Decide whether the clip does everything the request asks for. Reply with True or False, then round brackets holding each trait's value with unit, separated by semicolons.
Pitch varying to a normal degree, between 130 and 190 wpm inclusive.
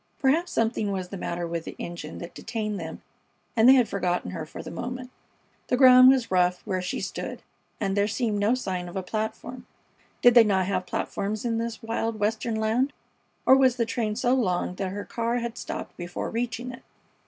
False (4.5 semitones; 200 wpm)